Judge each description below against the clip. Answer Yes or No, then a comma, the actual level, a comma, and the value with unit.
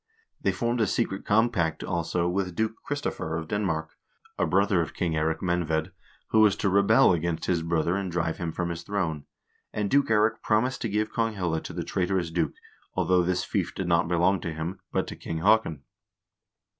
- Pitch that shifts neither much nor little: Yes, average, 4.1 semitones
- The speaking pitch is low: Yes, very low, 90 Hz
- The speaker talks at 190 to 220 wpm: Yes, average, 195 wpm